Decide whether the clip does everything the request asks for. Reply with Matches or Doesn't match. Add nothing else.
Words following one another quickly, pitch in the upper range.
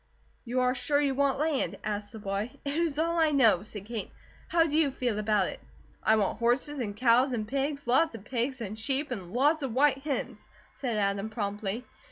Matches